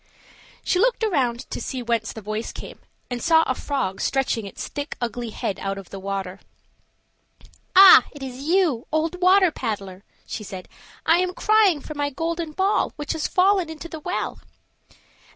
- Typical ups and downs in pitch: No, wide, 7.4 semitones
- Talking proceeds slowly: No, average, 170 wpm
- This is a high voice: Yes, very high, 285 Hz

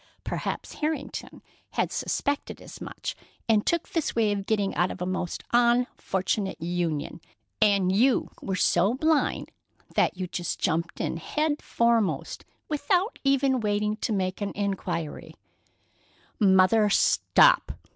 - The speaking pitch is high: Yes, high, 210 Hz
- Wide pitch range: Yes, wide, 5.7 semitones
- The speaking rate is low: Yes, slow, 130 wpm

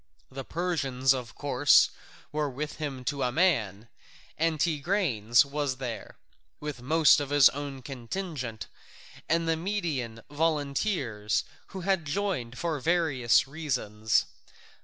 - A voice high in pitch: No, medium, 145 Hz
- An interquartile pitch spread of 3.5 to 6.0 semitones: Yes, average, 4.7 semitones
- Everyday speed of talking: No, slow, 115 wpm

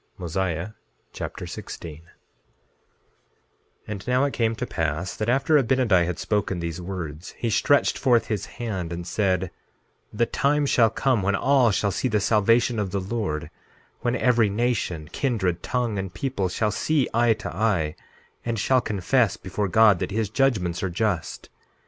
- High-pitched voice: No, low, 105 Hz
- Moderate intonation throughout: Yes, average, 4.6 semitones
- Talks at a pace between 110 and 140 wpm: No, average, 160 wpm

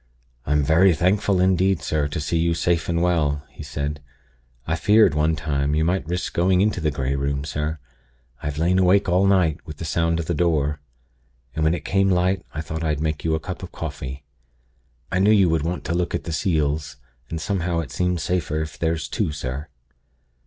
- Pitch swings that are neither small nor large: Yes, average, 3.0 semitones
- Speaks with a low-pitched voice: Yes, very low, 80 Hz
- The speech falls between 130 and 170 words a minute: No, fast, 205 wpm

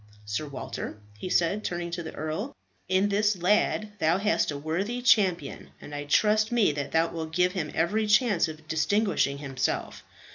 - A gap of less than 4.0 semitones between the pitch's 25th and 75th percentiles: No, average, 5.0 semitones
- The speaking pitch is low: No, medium, 175 Hz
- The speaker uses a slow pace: No, average, 175 wpm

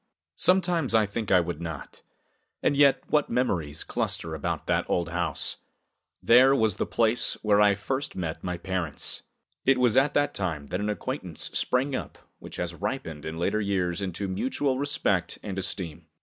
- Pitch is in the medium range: No, low, 100 Hz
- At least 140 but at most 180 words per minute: Yes, average, 170 wpm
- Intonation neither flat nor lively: No, wide, 6.6 semitones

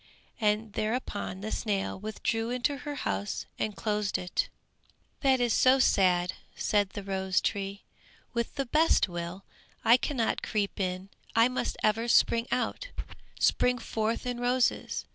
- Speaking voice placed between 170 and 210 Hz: No, high, 220 Hz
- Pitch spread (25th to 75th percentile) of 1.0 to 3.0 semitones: No, average, 3.9 semitones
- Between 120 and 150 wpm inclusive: Yes, average, 145 wpm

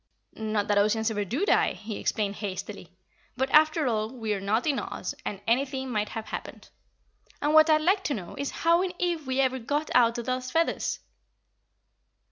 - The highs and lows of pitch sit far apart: Yes, wide, 6.0 semitones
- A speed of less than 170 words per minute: No, average, 190 wpm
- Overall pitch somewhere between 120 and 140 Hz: No, very high, 250 Hz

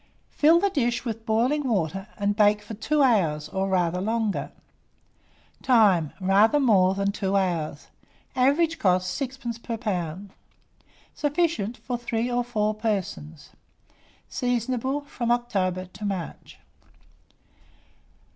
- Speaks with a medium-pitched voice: No, high, 215 Hz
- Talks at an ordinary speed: No, slow, 120 wpm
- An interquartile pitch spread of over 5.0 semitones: No, average, 4.4 semitones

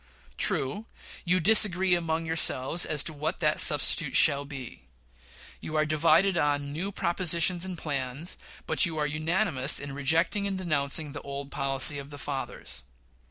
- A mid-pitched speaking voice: Yes, medium, 155 Hz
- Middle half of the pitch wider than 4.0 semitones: No, average, 3.5 semitones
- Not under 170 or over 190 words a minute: No, average, 155 wpm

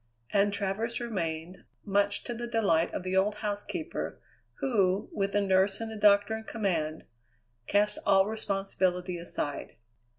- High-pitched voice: Yes, high, 200 Hz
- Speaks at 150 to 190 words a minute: No, average, 140 wpm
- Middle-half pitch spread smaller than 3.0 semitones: Yes, narrow, 2.4 semitones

